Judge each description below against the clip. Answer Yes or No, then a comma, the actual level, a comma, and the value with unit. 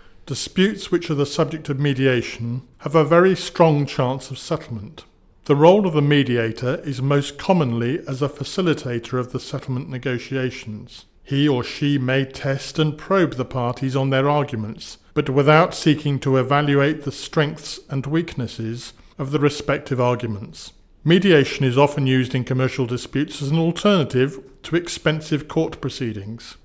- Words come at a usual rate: Yes, average, 155 wpm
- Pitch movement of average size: Yes, average, 3.2 semitones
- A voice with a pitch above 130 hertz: Yes, medium, 140 Hz